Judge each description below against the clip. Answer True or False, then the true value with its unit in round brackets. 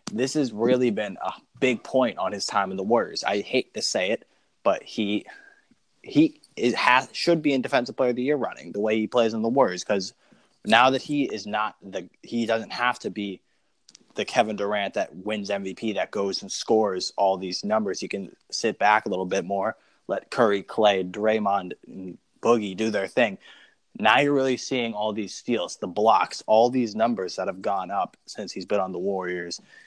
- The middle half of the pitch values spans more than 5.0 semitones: False (3.7 semitones)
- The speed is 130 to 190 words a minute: False (205 wpm)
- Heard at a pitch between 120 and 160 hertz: False (110 Hz)